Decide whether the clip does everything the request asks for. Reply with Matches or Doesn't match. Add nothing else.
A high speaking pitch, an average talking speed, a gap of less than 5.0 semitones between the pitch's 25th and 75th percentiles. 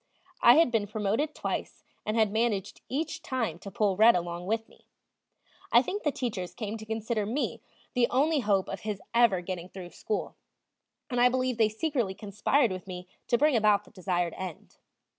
Matches